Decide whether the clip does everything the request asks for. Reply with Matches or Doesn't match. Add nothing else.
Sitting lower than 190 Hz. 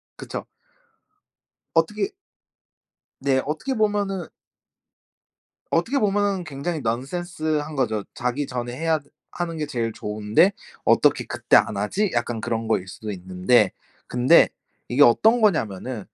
Matches